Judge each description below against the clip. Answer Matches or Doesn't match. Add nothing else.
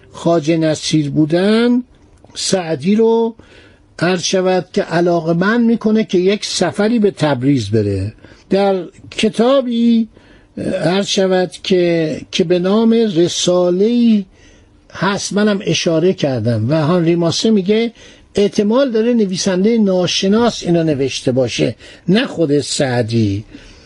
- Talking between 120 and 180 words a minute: Doesn't match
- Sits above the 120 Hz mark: Matches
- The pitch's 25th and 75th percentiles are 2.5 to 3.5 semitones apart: Doesn't match